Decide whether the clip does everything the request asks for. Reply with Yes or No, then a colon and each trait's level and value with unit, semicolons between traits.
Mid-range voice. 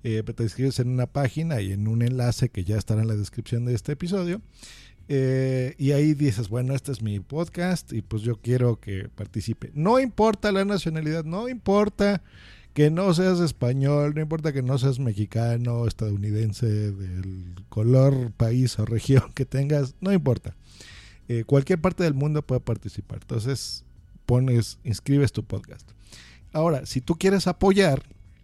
No: low, 125 Hz